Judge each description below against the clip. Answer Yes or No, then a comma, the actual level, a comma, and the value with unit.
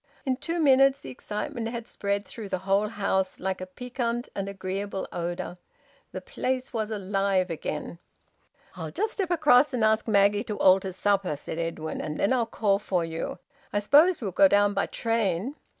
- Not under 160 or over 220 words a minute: Yes, average, 180 wpm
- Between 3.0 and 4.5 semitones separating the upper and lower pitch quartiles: Yes, average, 4.1 semitones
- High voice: Yes, high, 205 Hz